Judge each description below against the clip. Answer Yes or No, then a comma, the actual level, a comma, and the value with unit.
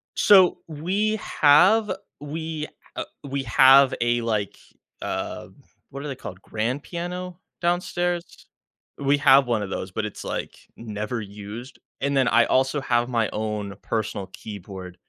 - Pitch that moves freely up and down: Yes, wide, 6.6 semitones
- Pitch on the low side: Yes, low, 130 Hz